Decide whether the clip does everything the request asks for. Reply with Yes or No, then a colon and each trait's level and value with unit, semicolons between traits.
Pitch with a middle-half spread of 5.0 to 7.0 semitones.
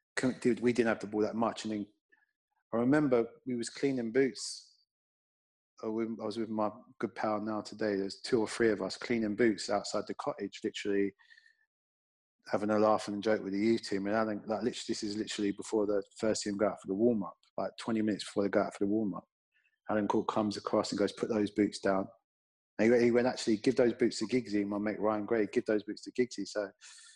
No: narrow, 2.5 semitones